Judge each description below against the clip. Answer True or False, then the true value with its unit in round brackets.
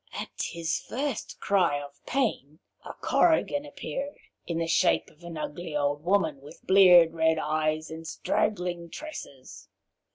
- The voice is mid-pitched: True (170 Hz)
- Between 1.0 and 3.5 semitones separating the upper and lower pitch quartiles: False (4.3 semitones)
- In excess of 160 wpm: False (140 wpm)